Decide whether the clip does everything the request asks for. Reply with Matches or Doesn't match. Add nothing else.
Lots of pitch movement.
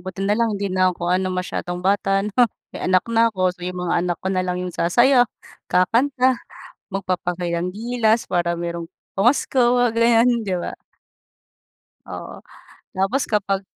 Doesn't match